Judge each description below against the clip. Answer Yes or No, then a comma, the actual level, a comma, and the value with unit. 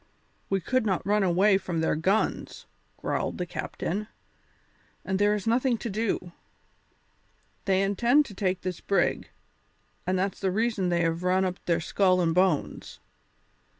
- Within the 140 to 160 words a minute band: Yes, average, 150 wpm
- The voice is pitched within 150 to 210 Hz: Yes, high, 190 Hz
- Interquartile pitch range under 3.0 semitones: Yes, narrow, 2.5 semitones